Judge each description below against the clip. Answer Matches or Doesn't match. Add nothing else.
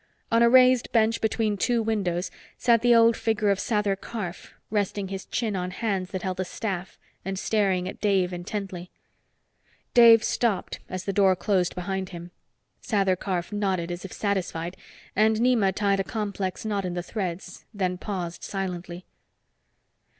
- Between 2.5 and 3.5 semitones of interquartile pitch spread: Matches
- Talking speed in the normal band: Matches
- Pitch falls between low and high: Doesn't match